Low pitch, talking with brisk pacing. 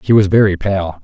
Yes: very low, 95 Hz; fast, 230 wpm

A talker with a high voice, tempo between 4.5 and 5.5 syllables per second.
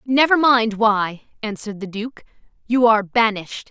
Yes: high, 220 Hz; 5.1 syllables/s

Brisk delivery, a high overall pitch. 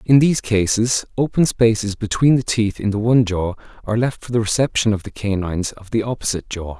No: fast, 210 wpm; low, 110 Hz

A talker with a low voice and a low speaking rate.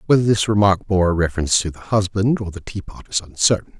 No: very low, 95 Hz; fast, 205 wpm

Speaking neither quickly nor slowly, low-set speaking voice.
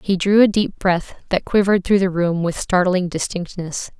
No: average, 195 wpm; medium, 185 Hz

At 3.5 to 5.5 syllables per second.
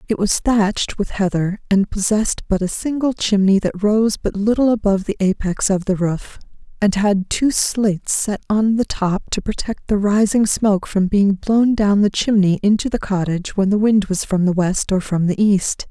Yes: 4.8 syllables/s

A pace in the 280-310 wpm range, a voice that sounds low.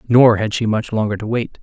No: fast, 260 wpm; low, 110 Hz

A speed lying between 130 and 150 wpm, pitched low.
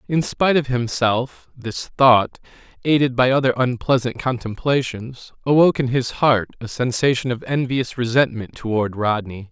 Yes: average, 140 wpm; low, 125 Hz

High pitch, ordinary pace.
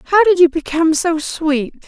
Yes: very high, 325 Hz; average, 190 wpm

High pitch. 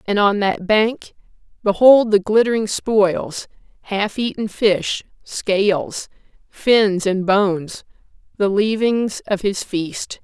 Yes: high, 205 Hz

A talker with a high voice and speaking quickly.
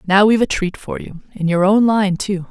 Yes: high, 195 Hz; fast, 265 wpm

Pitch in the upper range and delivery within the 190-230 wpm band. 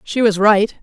Yes: high, 210 Hz; fast, 220 wpm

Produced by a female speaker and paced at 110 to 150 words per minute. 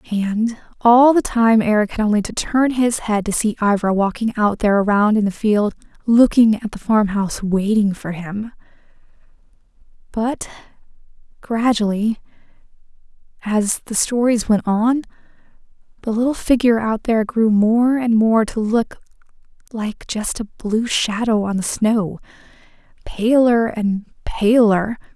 Yes: female; average, 140 wpm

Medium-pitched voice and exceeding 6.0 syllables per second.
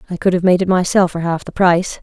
Yes: medium, 180 Hz; 6.6 syllables/s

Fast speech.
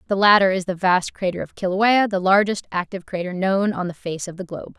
Yes: fast, 240 wpm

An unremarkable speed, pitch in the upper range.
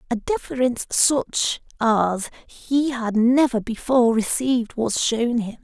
No: slow, 130 wpm; high, 240 Hz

